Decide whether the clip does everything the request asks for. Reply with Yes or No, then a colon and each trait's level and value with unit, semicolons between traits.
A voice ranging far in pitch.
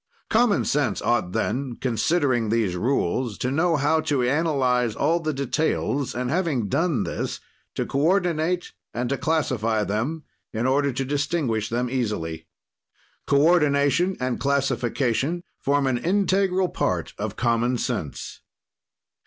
No: average, 4.9 semitones